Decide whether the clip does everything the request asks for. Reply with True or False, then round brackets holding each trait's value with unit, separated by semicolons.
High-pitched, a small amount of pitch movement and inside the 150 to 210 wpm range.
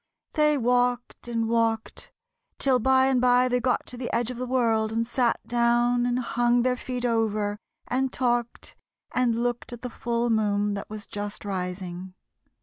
True (240 Hz; 2.0 semitones; 170 wpm)